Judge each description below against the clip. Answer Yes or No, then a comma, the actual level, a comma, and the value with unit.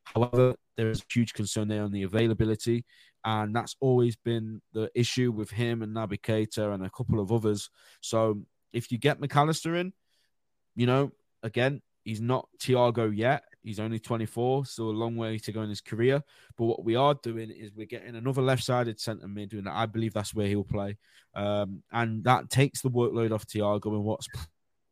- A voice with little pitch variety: Yes, narrow, 2.3 semitones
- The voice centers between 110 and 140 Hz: Yes, low, 115 Hz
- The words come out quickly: No, average, 190 wpm